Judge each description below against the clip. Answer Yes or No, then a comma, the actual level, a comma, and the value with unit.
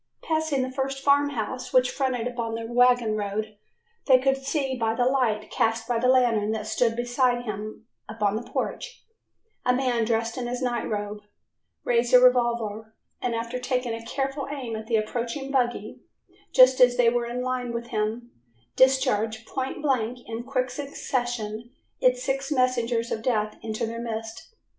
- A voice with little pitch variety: Yes, narrow, 2.3 semitones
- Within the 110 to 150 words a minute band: No, average, 170 wpm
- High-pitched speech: Yes, high, 240 Hz